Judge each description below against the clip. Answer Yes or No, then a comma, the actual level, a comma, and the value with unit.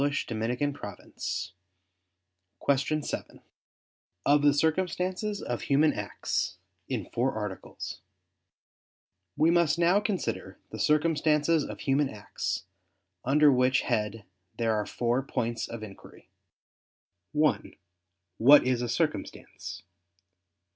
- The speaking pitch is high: No, medium, 140 Hz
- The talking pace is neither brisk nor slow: No, slow, 100 wpm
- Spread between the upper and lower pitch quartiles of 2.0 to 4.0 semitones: No, average, 4.8 semitones